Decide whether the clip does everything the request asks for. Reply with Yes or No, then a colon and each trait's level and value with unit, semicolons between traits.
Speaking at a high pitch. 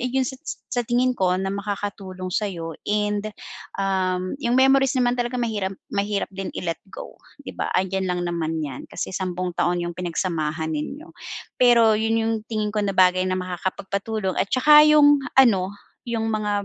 Yes: high, 200 Hz